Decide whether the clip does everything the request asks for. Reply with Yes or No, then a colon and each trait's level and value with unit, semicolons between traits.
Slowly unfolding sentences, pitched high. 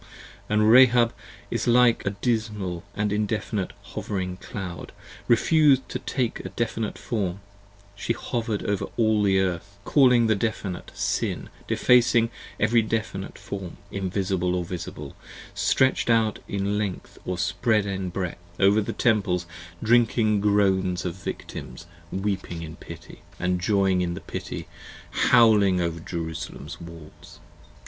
No: slow, 130 wpm; low, 100 Hz